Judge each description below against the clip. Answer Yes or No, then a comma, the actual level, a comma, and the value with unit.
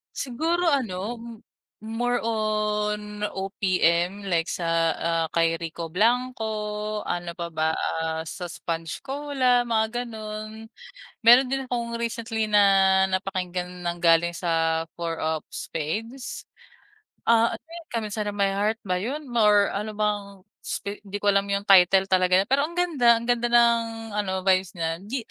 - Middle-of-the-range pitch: No, high, 210 Hz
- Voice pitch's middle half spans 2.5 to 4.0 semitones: No, average, 4.6 semitones